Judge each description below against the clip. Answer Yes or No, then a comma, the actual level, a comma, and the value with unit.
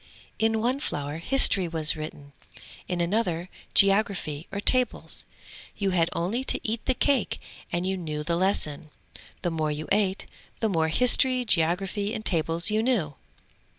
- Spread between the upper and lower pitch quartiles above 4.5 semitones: Yes, average, 5.2 semitones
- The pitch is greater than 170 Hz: Yes, medium, 185 Hz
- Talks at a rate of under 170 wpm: Yes, average, 150 wpm